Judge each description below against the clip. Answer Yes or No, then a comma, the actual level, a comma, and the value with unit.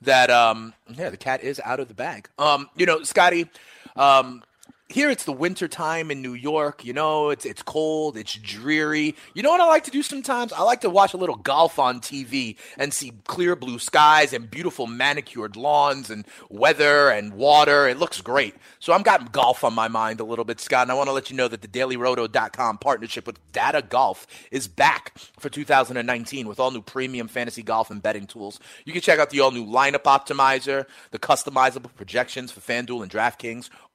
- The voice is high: No, low, 135 Hz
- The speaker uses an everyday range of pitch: Yes, average, 4.1 semitones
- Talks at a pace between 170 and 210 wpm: Yes, fast, 205 wpm